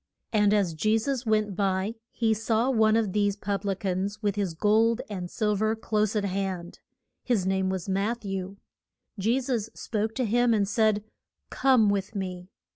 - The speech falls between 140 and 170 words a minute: No, average, 180 wpm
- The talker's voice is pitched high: Yes, high, 210 Hz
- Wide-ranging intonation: No, narrow, 2.4 semitones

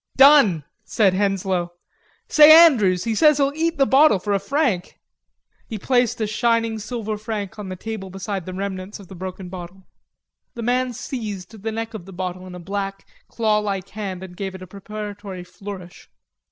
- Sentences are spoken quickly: No, average, 180 wpm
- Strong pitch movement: No, average, 3.4 semitones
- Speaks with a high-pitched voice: Yes, high, 205 Hz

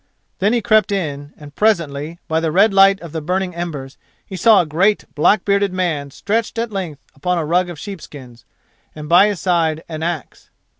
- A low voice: No, medium, 175 Hz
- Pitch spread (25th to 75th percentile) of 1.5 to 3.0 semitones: No, average, 4.4 semitones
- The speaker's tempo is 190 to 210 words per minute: Yes, average, 195 wpm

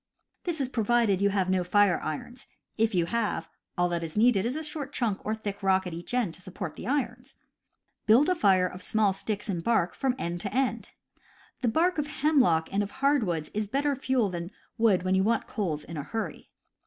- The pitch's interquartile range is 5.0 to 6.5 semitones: Yes, wide, 5.4 semitones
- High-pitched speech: Yes, high, 210 Hz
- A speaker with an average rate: No, fast, 215 wpm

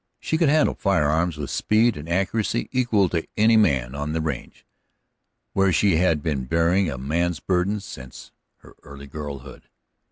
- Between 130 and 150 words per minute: No, average, 160 wpm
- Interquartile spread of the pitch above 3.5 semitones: Yes, average, 5.3 semitones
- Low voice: Yes, very low, 85 Hz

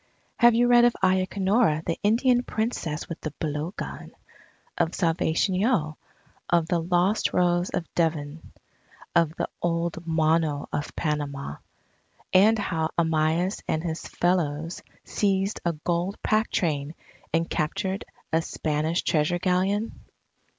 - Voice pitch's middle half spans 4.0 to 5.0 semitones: No, average, 3.3 semitones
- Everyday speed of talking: No, slow, 125 wpm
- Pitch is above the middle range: No, medium, 170 Hz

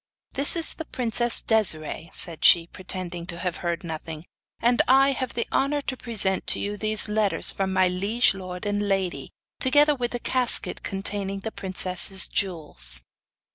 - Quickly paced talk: No, average, 165 wpm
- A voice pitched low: No, high, 195 Hz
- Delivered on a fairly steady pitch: No, average, 4.9 semitones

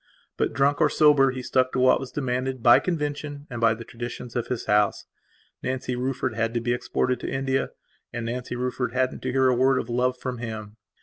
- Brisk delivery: Yes, fast, 210 wpm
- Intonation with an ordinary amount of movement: No, narrow, 1.8 semitones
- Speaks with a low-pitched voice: Yes, low, 125 Hz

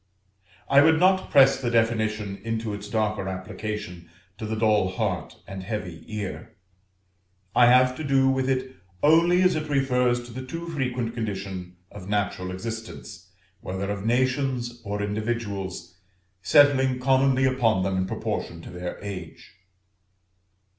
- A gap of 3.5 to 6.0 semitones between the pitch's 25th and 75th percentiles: Yes, average, 4.8 semitones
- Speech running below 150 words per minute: Yes, average, 140 wpm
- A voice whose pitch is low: Yes, low, 115 Hz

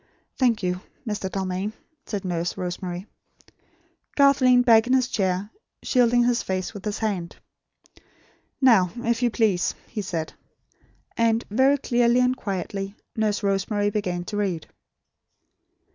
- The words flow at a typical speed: No, slow, 130 wpm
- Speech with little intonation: No, average, 4.2 semitones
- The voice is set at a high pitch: Yes, high, 210 Hz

